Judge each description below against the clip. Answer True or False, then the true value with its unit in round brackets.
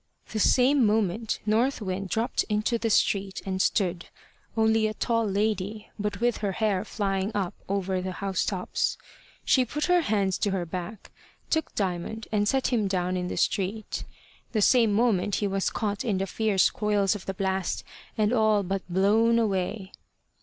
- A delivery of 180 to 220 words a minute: False (170 wpm)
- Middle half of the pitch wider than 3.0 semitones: False (2.6 semitones)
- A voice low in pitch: False (205 Hz)